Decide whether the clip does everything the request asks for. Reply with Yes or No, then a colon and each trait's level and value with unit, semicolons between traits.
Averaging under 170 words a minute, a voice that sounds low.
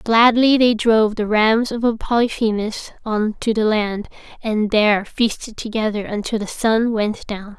No: average, 160 wpm; high, 220 Hz